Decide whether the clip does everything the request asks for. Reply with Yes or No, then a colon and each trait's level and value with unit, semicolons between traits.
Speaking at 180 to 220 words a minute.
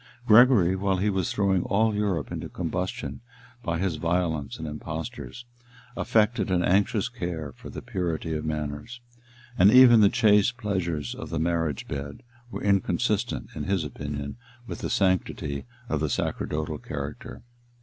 No: average, 150 wpm